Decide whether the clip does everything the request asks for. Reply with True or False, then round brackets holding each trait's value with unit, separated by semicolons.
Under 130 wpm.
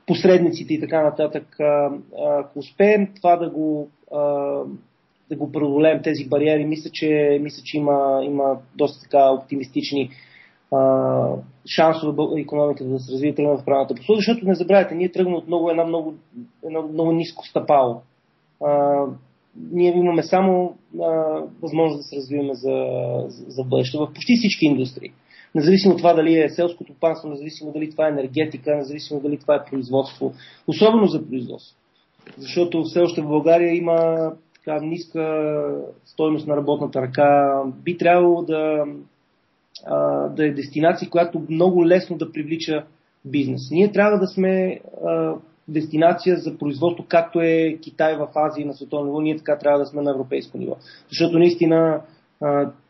False (150 wpm)